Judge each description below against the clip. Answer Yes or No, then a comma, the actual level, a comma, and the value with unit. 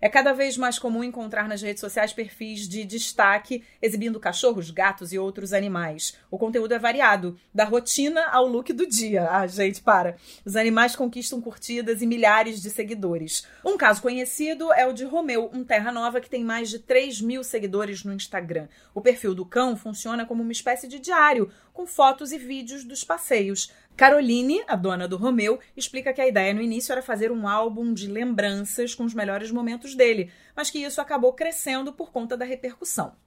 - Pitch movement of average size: Yes, average, 3.8 semitones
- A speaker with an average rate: No, fast, 190 wpm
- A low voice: No, high, 235 Hz